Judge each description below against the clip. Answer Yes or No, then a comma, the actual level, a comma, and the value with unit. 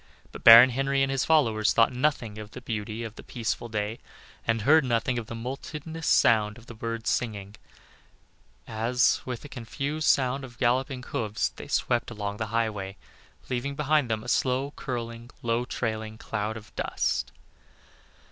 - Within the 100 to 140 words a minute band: No, average, 165 wpm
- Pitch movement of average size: Yes, average, 3.0 semitones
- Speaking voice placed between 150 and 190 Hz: No, low, 120 Hz